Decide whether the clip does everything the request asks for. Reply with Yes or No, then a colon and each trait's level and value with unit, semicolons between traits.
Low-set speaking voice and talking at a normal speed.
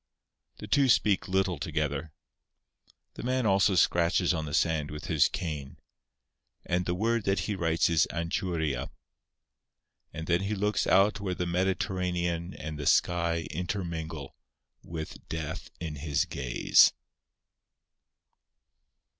No: very low, 85 Hz; slow, 125 wpm